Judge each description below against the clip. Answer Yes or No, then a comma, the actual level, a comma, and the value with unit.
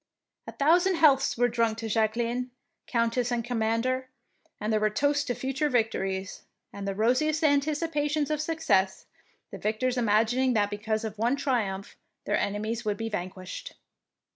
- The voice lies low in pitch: No, high, 235 Hz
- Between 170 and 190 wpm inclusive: No, average, 155 wpm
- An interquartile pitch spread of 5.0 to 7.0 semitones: No, average, 4.6 semitones